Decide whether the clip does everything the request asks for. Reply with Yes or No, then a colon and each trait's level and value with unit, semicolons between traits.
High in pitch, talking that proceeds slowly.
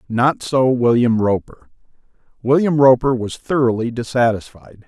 No: low, 125 Hz; slow, 110 wpm